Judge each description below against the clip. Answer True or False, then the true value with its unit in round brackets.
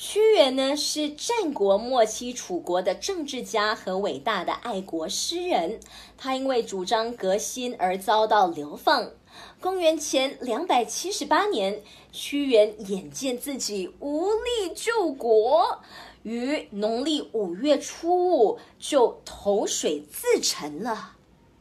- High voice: True (250 Hz)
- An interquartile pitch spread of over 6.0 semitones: True (7.2 semitones)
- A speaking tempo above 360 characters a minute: False (185 characters per minute)